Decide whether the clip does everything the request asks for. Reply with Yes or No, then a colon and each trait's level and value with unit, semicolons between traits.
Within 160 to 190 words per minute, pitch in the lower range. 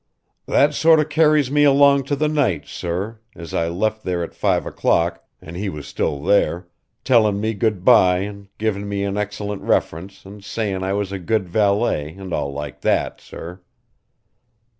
Yes: average, 175 wpm; low, 100 Hz